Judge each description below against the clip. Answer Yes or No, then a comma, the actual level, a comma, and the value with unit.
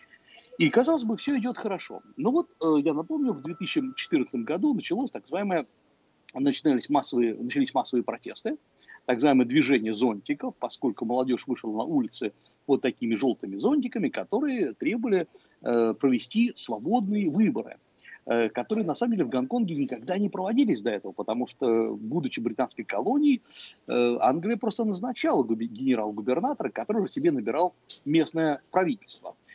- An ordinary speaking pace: Yes, average, 130 wpm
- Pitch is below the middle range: No, high, 200 Hz